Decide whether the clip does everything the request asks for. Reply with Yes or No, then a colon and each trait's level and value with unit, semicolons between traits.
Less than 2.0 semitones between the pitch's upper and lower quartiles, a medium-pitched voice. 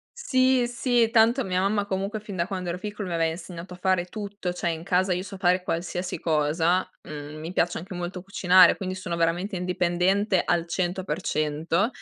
No: narrow, 2.4 semitones; medium, 180 Hz